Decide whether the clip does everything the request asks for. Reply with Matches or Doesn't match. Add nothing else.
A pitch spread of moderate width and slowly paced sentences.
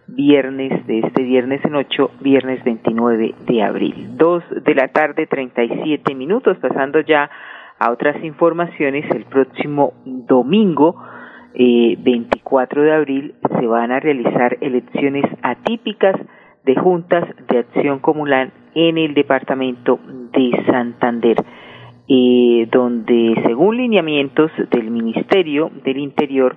Matches